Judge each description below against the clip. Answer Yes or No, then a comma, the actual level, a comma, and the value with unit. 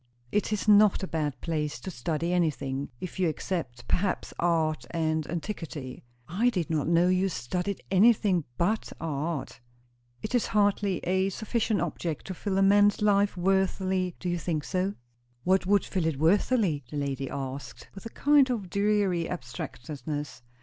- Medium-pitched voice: Yes, medium, 180 Hz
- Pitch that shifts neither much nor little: Yes, average, 4.3 semitones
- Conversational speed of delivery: Yes, average, 160 wpm